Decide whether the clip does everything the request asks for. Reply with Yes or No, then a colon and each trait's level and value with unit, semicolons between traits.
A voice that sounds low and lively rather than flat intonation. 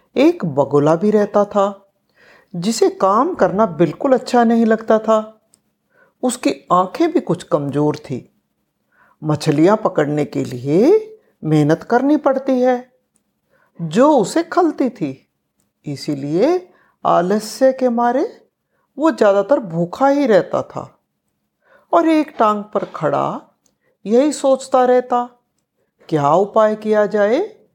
No: high, 220 Hz; wide, 7.6 semitones